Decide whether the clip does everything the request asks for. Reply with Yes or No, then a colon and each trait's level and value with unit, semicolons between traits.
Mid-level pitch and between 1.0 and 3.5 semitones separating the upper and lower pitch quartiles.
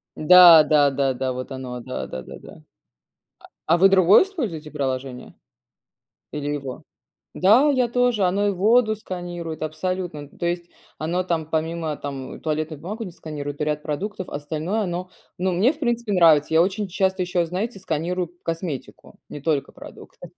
No: medium, 170 Hz; average, 4.1 semitones